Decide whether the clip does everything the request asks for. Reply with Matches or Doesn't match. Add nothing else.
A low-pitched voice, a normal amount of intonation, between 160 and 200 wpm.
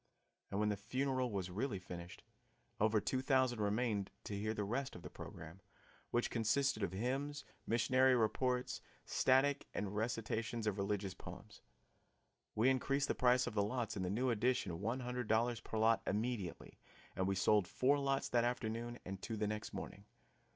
Matches